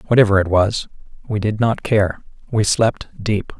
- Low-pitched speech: Yes, low, 105 Hz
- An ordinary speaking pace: Yes, average, 165 wpm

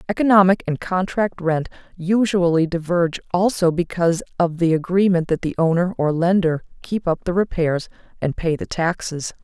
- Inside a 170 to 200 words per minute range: No, average, 155 wpm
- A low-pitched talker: No, medium, 175 Hz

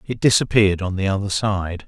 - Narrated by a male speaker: Yes, male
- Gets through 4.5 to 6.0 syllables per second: Yes, 5.7 syllables/s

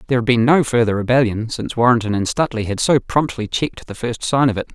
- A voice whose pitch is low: Yes, low, 120 Hz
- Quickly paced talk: Yes, fast, 240 wpm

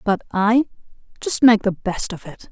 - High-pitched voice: Yes, high, 215 Hz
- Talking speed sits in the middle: Yes, average, 190 wpm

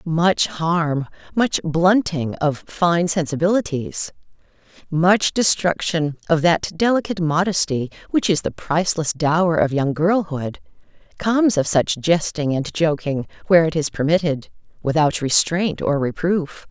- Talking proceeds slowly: Yes, slow, 125 wpm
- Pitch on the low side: No, medium, 165 Hz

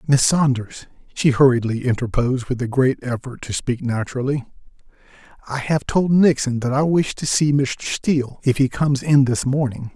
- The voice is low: Yes, low, 130 Hz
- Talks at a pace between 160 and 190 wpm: Yes, average, 175 wpm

